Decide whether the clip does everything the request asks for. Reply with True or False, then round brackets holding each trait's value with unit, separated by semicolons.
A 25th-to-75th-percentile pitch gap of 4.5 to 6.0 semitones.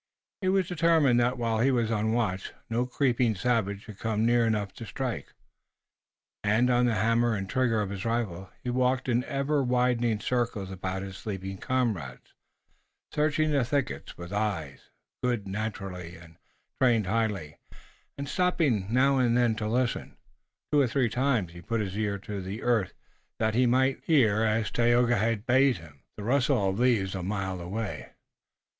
False (4.0 semitones)